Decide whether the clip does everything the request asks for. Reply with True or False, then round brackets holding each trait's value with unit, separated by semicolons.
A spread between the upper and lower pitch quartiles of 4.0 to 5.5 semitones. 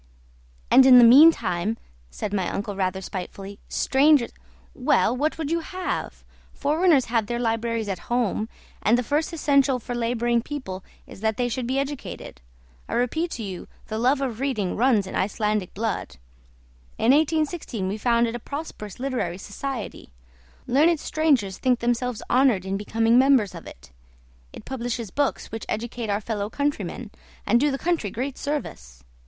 True (4.8 semitones)